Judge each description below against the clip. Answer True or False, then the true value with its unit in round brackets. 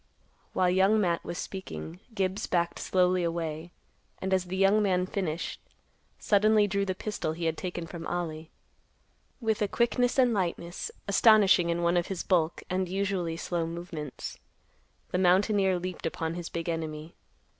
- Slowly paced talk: False (155 wpm)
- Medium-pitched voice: True (180 Hz)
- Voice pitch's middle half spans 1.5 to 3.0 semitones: True (2.6 semitones)